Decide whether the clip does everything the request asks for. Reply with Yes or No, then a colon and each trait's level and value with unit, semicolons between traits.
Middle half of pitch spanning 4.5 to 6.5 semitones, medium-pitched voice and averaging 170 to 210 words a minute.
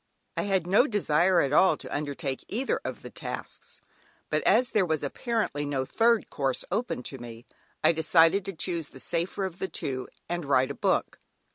Yes: wide, 5.6 semitones; medium, 165 Hz; average, 185 wpm